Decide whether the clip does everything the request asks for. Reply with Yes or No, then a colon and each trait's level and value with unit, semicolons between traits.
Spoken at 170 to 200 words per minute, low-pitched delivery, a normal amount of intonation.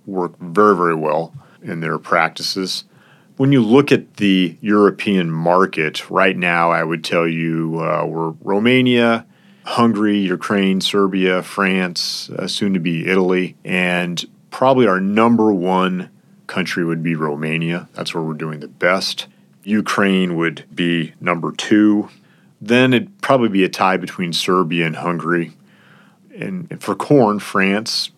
No: average, 145 wpm; very low, 95 Hz; average, 4.1 semitones